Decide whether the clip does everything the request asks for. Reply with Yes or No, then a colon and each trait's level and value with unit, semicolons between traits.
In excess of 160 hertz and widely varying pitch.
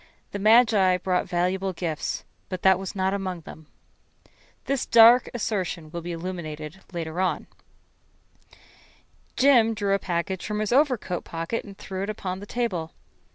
No: high, 190 Hz; average, 3.5 semitones